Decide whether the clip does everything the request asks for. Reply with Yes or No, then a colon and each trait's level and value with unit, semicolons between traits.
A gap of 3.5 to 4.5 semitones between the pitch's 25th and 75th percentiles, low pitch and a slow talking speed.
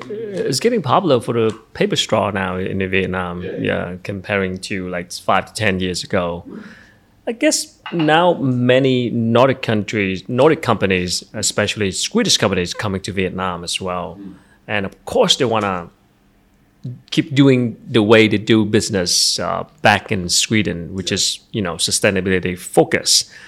Yes: average, 3.8 semitones; low, 100 Hz; slow, 150 wpm